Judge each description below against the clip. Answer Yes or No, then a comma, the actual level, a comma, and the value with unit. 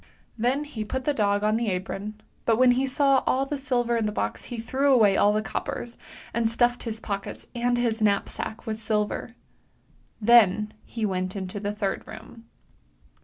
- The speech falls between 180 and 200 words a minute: Yes, average, 185 wpm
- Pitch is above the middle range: Yes, high, 225 Hz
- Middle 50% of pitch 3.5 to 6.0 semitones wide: No, average, 2.7 semitones